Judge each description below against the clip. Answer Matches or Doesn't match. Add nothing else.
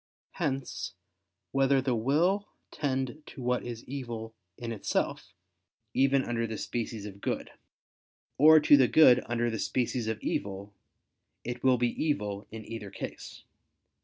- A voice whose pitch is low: Matches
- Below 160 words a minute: Matches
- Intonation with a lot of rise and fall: Doesn't match